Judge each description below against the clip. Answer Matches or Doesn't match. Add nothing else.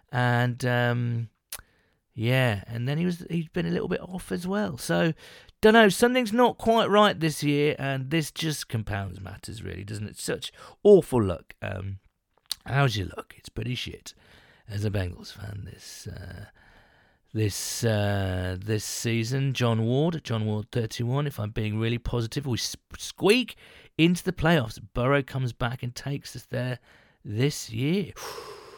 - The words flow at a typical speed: Matches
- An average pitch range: Doesn't match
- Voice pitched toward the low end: Matches